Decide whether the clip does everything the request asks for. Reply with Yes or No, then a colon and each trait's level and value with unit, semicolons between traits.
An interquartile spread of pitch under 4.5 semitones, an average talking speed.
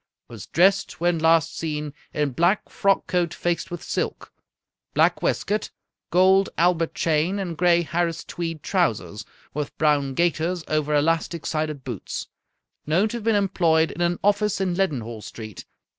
Yes: average, 3.1 semitones; average, 150 wpm